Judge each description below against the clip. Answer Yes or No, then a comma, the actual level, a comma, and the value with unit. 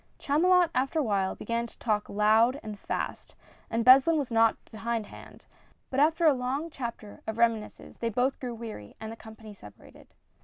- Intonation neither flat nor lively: Yes, average, 3.6 semitones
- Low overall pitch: No, high, 235 Hz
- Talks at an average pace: Yes, average, 180 wpm